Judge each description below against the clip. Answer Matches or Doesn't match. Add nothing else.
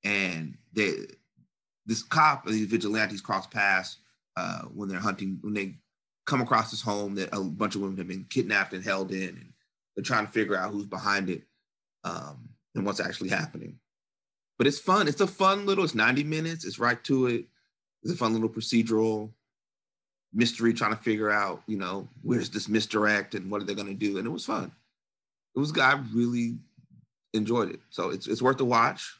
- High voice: Doesn't match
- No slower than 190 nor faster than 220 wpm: Matches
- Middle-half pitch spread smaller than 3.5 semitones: Matches